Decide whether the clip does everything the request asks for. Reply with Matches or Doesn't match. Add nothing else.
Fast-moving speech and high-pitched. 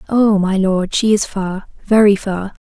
Doesn't match